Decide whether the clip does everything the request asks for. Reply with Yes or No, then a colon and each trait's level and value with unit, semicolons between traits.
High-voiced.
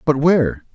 No: low, 135 Hz